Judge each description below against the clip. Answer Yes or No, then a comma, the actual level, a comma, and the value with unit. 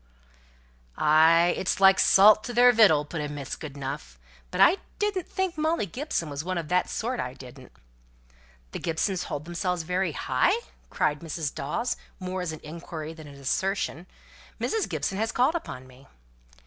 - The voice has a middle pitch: Yes, medium, 170 Hz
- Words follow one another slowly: No, average, 165 wpm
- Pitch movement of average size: No, wide, 6.2 semitones